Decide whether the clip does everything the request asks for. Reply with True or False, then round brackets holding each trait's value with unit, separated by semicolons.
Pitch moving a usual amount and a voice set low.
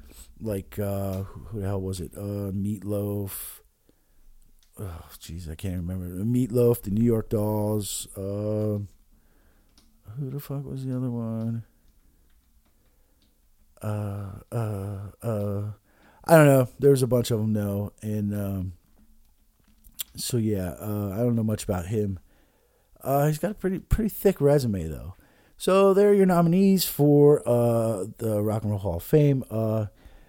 True (3.8 semitones; 105 Hz)